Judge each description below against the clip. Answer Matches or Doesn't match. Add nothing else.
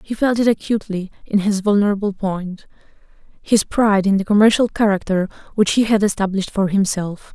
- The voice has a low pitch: Doesn't match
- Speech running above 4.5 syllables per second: Matches